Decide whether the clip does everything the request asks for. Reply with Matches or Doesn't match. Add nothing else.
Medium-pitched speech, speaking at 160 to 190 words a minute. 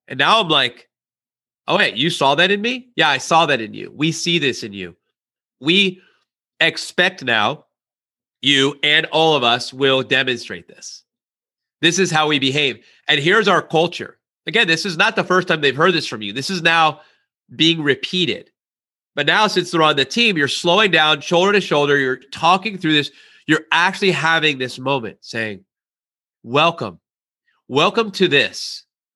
Matches